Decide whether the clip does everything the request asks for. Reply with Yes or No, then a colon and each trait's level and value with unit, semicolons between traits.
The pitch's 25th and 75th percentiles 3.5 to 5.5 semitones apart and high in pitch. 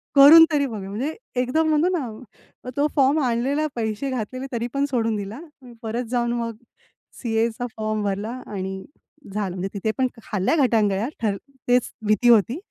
Yes: average, 3.8 semitones; high, 235 Hz